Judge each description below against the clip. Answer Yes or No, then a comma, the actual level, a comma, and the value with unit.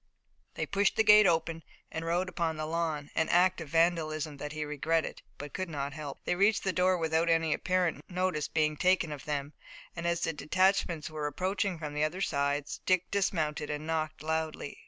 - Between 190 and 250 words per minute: Yes, average, 195 wpm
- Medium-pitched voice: Yes, medium, 160 Hz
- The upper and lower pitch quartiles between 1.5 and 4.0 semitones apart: Yes, average, 3.0 semitones